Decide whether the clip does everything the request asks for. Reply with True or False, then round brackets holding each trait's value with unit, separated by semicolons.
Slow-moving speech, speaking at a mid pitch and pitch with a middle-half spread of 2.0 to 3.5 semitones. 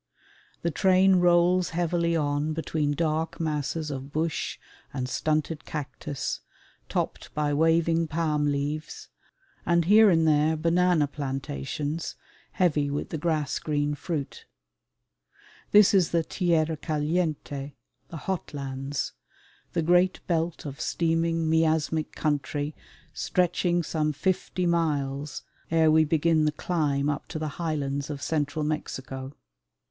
True (120 wpm; 155 Hz; 2.4 semitones)